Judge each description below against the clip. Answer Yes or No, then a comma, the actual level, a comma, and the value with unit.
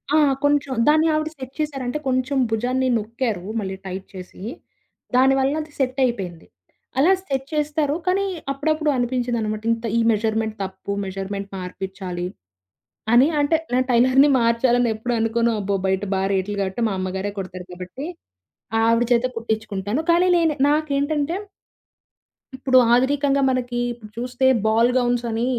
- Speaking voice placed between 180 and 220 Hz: No, high, 240 Hz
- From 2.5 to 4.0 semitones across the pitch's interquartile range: No, average, 4.9 semitones